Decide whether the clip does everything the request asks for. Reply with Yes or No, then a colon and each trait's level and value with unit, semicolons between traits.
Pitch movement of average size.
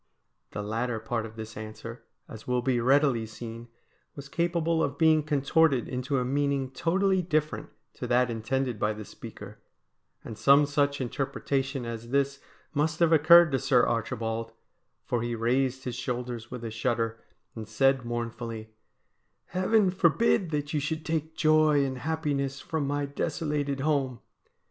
Yes: average, 4.3 semitones